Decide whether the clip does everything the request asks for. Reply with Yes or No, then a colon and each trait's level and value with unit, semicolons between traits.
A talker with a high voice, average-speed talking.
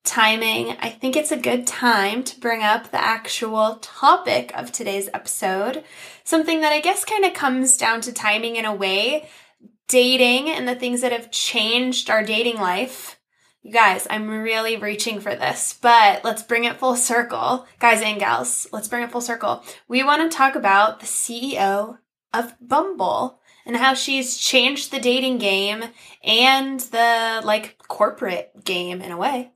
Yes: high, 235 Hz; average, 170 wpm